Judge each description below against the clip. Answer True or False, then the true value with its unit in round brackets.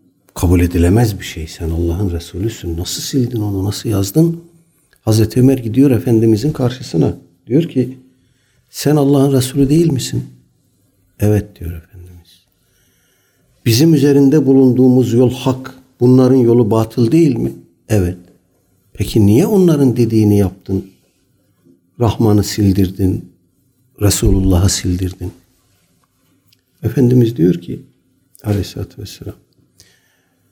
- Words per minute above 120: False (100 wpm)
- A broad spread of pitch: True (5.7 semitones)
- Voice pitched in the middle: False (110 Hz)